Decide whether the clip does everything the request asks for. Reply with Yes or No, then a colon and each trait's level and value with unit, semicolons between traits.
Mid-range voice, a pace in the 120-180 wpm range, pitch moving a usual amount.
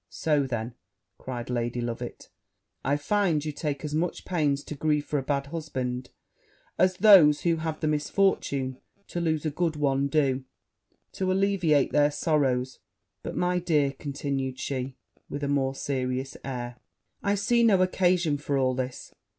Yes: medium, 145 Hz; average, 160 wpm; average, 3.8 semitones